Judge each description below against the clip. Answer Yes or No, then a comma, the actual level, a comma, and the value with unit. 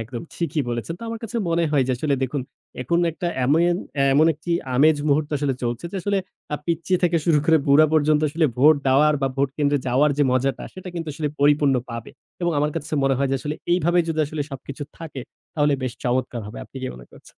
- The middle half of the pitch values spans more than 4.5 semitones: No, average, 3.4 semitones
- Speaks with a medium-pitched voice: Yes, medium, 150 Hz